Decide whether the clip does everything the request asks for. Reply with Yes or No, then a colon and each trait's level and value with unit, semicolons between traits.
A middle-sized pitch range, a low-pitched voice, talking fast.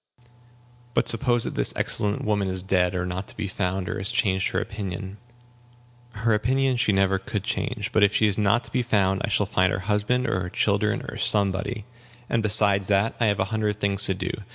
No: narrow, 2.3 semitones; low, 100 Hz; fast, 215 wpm